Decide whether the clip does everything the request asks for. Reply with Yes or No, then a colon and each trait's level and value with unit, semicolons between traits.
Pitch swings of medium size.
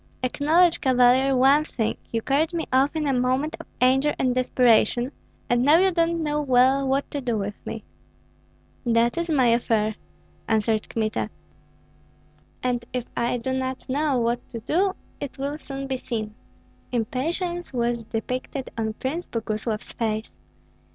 Yes: average, 3.5 semitones